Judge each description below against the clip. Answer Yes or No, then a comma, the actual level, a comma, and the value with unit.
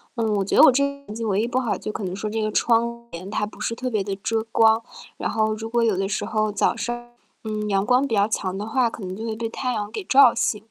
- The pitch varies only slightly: Yes, narrow, 2.2 semitones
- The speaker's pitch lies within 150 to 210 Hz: No, high, 220 Hz